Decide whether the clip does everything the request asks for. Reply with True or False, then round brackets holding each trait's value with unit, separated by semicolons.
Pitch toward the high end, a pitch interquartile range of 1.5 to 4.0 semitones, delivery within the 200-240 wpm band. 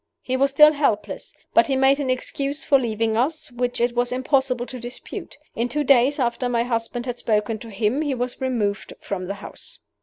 True (245 Hz; 2.7 semitones; 205 wpm)